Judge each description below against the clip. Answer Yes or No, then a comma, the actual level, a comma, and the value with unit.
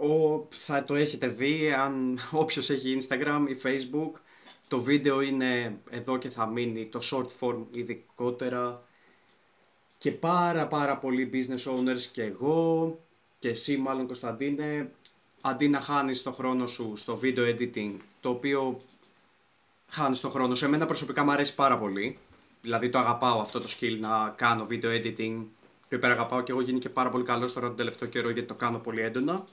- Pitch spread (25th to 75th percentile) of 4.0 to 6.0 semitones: No, average, 2.8 semitones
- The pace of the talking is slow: No, fast, 170 wpm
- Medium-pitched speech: No, low, 130 Hz